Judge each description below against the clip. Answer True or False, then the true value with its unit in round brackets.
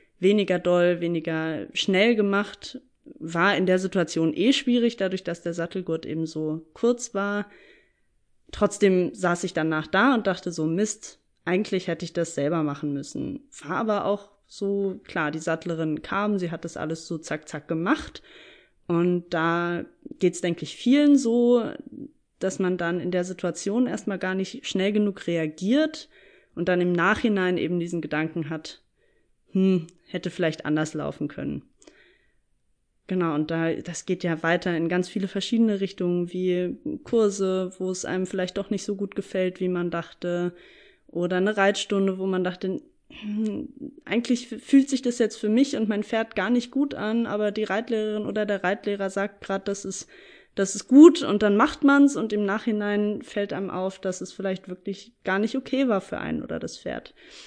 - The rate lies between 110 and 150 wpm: False (175 wpm)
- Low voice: False (195 Hz)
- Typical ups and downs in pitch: True (3.9 semitones)